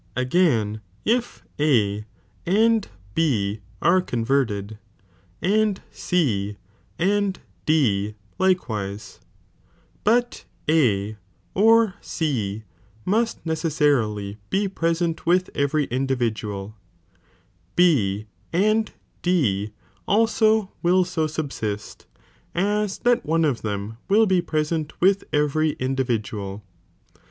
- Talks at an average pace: No, slow, 90 wpm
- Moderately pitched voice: Yes, medium, 155 Hz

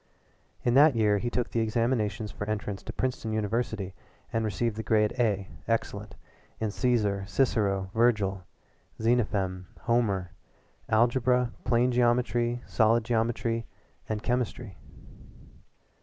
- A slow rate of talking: Yes, slow, 115 wpm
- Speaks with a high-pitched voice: No, low, 115 Hz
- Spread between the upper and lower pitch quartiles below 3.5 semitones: Yes, narrow, 2.5 semitones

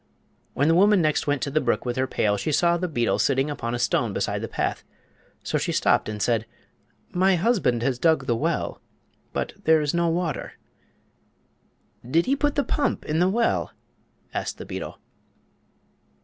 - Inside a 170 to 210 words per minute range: Yes, average, 180 wpm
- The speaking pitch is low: No, medium, 155 Hz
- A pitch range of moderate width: No, wide, 6.1 semitones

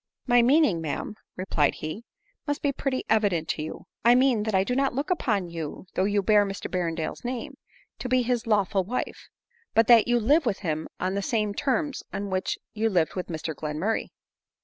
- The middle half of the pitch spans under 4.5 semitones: No, average, 5.2 semitones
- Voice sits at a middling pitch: No, high, 210 Hz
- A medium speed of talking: No, fast, 210 wpm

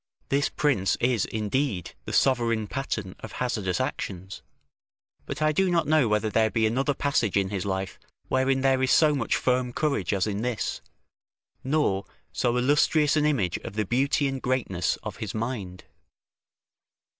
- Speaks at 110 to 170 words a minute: Yes, average, 160 wpm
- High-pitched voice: No, low, 125 Hz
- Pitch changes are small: No, average, 5.2 semitones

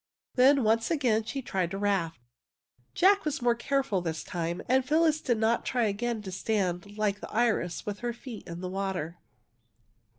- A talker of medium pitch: No, high, 220 Hz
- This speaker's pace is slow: No, average, 175 wpm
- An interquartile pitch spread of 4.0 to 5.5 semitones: Yes, average, 4.9 semitones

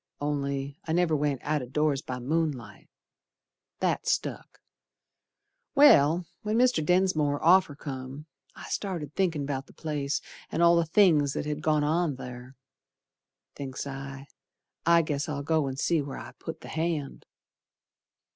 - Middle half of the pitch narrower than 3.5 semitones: Yes, average, 3.1 semitones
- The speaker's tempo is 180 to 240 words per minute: No, average, 145 wpm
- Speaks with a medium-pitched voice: Yes, medium, 150 Hz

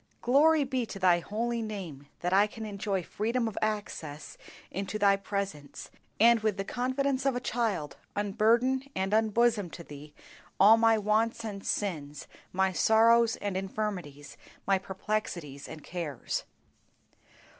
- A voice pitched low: No, high, 205 Hz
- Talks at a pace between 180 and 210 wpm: No, average, 140 wpm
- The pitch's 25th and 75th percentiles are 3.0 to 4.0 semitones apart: Yes, average, 3.6 semitones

